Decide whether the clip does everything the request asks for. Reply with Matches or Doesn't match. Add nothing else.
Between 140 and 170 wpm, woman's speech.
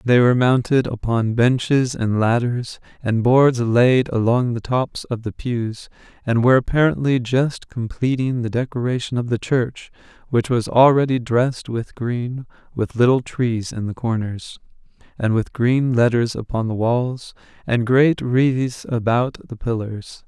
Doesn't match